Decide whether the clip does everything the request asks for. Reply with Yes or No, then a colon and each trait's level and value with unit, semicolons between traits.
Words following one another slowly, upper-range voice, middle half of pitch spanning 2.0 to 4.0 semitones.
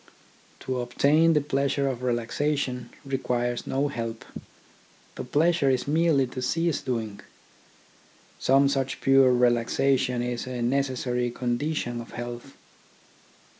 No: slow, 120 wpm; low, 130 Hz; narrow, 2.4 semitones